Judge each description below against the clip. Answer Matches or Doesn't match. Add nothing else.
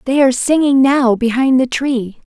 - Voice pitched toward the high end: Matches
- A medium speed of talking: Matches